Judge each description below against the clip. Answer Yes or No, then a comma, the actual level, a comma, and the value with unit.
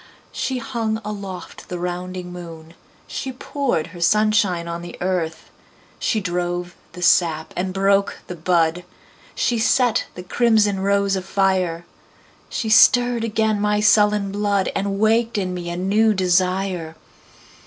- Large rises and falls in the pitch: No, average, 3.2 semitones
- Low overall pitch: No, high, 190 Hz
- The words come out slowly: Yes, slow, 120 wpm